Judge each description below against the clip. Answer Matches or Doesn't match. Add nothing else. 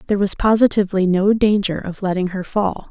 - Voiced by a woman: Matches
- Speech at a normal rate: Matches